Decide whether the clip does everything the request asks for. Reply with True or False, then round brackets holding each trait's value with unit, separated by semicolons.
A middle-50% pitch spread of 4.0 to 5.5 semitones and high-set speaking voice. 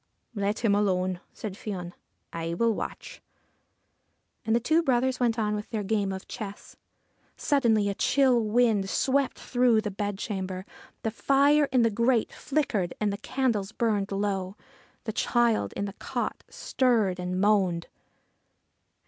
False (3.5 semitones; 215 Hz)